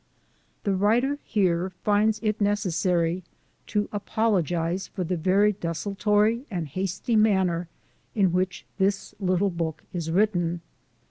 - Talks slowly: Yes, slow, 120 wpm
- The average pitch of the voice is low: No, high, 190 Hz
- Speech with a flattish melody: No, average, 3.1 semitones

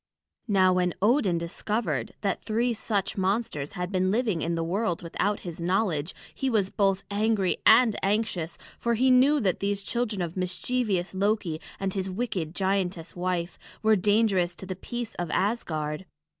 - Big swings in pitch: No, average, 3.6 semitones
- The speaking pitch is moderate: No, high, 195 Hz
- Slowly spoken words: No, average, 160 wpm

